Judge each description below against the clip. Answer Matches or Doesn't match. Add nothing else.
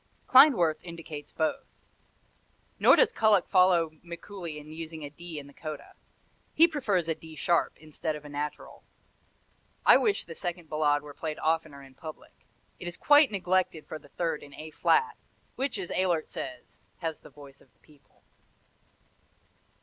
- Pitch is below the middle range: Doesn't match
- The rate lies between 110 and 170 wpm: Matches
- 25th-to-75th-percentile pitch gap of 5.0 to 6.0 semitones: Doesn't match